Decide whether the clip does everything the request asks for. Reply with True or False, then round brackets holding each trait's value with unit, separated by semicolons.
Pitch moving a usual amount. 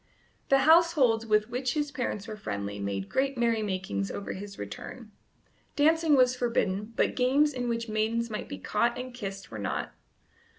True (4.5 semitones)